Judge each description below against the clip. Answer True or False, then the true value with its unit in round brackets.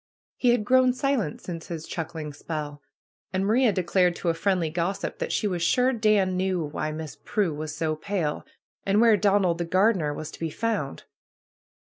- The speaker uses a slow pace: False (190 wpm)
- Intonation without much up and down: False (4.7 semitones)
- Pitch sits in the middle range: True (180 Hz)